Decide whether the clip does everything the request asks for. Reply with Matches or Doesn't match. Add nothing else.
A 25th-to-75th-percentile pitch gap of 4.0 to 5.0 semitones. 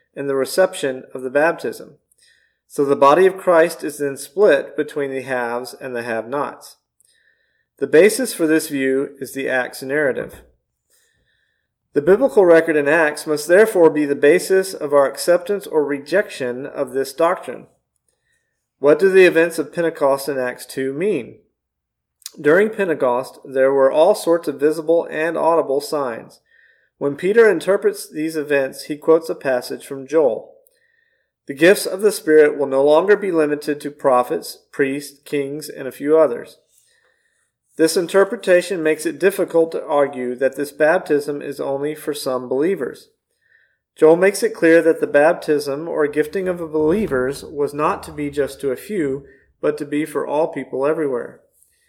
Matches